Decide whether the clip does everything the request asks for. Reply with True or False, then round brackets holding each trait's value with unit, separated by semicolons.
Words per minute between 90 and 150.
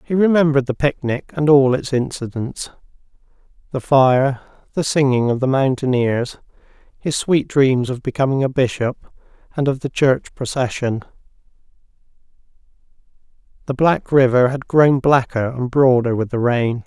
True (135 wpm)